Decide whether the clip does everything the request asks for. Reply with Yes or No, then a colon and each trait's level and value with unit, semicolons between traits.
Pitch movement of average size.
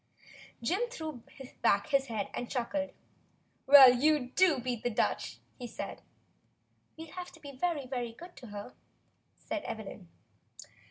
Yes: average, 4.7 semitones